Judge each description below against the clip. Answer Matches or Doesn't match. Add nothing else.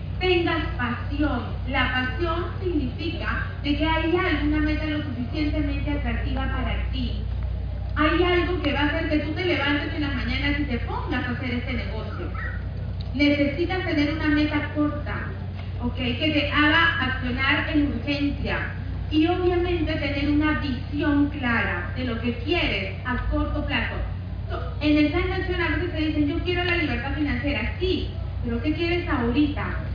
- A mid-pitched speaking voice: Doesn't match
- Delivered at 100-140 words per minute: Doesn't match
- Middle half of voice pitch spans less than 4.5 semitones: Doesn't match